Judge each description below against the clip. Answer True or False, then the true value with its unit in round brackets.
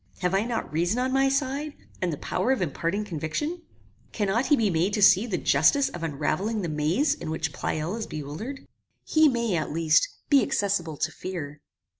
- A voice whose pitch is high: True (195 Hz)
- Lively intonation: True (7.7 semitones)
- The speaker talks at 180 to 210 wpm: True (190 wpm)